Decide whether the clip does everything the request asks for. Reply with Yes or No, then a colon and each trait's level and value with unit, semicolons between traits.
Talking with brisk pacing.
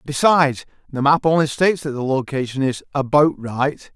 No: average, 165 wpm